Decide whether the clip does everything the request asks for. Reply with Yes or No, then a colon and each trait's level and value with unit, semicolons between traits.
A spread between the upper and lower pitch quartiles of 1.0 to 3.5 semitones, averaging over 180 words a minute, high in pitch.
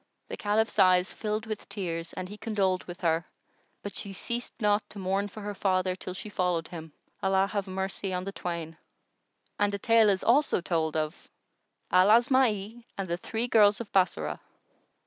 No: narrow, 2.6 semitones; average, 175 wpm; high, 195 Hz